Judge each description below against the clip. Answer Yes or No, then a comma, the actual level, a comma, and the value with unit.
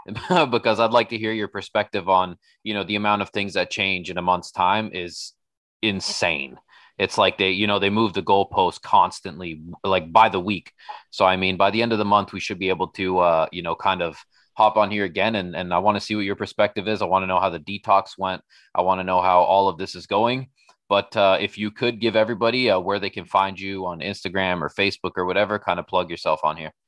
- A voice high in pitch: No, low, 100 Hz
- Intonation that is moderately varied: No, narrow, 2.1 semitones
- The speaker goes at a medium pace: No, fast, 250 wpm